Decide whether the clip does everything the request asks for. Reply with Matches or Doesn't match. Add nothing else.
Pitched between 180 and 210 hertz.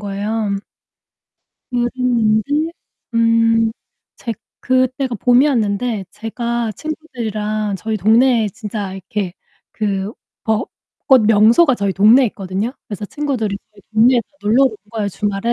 Doesn't match